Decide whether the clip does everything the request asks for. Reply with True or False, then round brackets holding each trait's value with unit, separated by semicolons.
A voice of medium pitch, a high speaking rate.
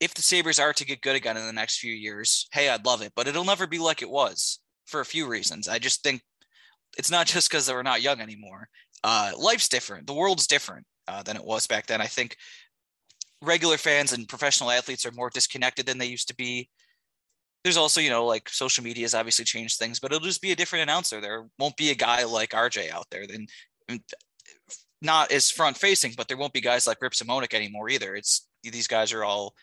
False (125 Hz; 230 wpm)